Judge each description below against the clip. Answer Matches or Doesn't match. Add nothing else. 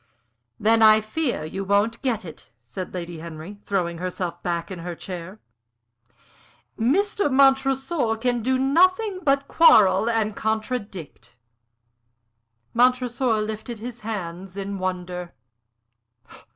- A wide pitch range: Matches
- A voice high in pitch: Matches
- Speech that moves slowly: Matches